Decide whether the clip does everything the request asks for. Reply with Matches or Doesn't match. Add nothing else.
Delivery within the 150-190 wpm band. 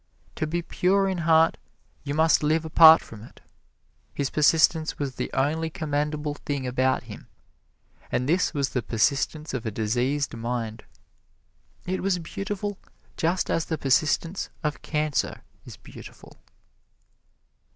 Doesn't match